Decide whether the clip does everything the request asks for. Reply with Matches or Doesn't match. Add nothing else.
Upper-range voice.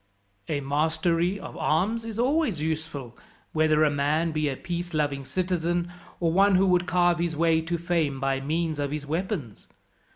Doesn't match